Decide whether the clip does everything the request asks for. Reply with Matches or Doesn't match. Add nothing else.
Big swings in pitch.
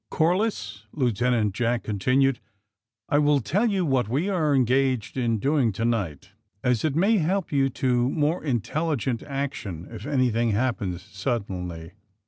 Doesn't match